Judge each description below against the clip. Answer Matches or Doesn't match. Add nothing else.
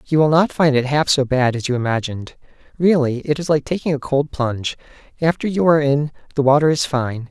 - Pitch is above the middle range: Doesn't match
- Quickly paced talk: Matches